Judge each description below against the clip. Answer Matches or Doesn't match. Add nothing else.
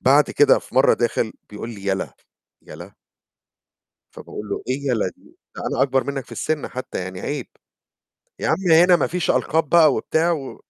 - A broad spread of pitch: Matches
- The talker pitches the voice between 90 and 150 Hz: Matches